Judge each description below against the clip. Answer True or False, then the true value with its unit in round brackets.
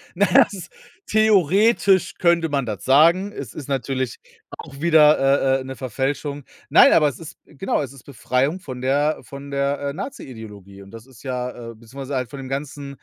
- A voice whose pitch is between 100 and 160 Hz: True (140 Hz)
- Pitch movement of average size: True (3.5 semitones)